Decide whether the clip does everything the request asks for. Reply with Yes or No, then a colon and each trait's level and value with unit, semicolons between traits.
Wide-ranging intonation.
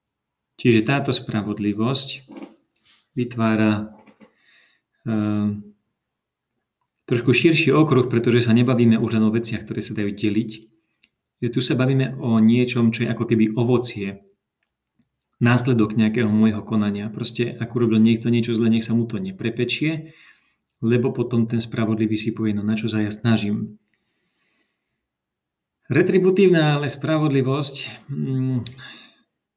No: narrow, 2.6 semitones